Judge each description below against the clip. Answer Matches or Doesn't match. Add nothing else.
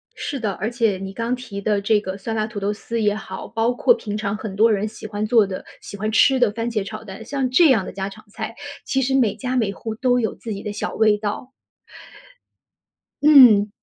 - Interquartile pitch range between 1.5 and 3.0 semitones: Matches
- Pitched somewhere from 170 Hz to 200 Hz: Doesn't match